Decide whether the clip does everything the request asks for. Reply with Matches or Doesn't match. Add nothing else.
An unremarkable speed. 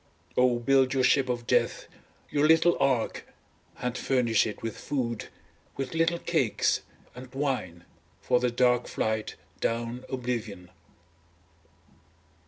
Doesn't match